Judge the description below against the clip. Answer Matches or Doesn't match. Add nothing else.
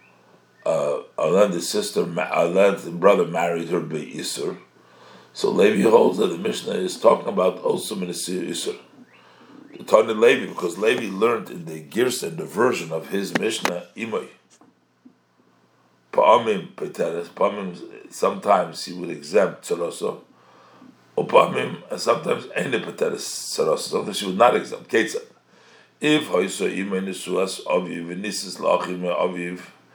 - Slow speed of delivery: Matches